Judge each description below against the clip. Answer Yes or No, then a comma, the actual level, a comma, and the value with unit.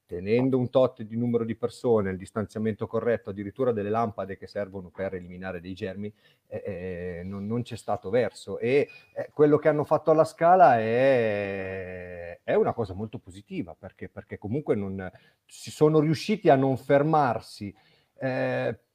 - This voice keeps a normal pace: Yes, average, 160 wpm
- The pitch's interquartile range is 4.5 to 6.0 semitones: Yes, average, 5.1 semitones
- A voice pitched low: Yes, low, 110 Hz